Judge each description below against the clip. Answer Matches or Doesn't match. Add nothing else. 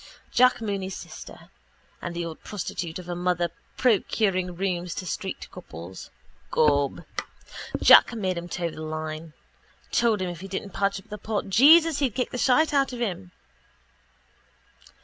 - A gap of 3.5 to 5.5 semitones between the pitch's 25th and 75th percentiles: Matches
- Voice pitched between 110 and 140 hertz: Doesn't match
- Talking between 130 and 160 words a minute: Matches